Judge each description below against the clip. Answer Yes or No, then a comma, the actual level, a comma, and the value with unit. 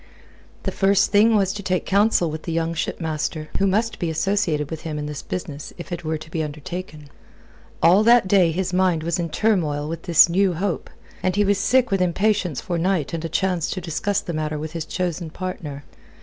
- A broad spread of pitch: No, average, 3.5 semitones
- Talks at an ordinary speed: No, fast, 210 wpm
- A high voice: No, medium, 175 Hz